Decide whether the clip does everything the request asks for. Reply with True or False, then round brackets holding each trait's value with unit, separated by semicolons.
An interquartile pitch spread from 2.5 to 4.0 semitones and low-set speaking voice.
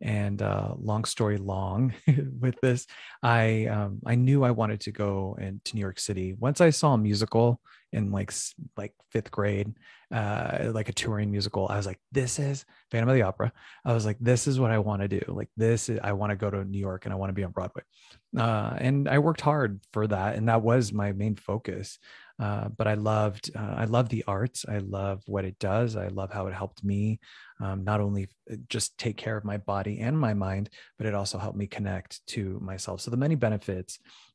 True (3.0 semitones; 105 Hz)